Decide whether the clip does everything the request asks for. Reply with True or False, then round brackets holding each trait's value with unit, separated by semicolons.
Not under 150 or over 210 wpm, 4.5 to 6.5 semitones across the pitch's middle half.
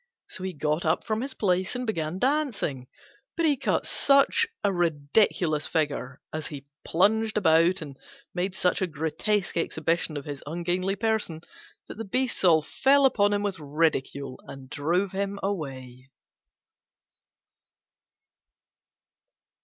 False (135 wpm; 5.2 semitones)